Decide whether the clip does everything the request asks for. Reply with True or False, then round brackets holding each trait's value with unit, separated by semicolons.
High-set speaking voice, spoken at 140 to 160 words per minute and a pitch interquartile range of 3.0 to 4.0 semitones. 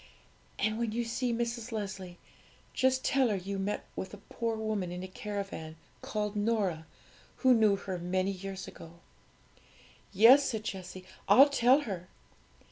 True (210 Hz; 150 wpm; 3.7 semitones)